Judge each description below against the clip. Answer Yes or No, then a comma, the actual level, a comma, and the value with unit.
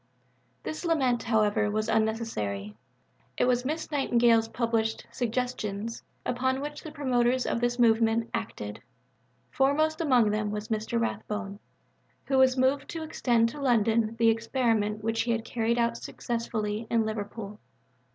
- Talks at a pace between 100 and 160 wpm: Yes, average, 140 wpm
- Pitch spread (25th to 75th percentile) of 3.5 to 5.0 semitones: No, narrow, 2.6 semitones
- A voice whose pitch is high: Yes, high, 230 Hz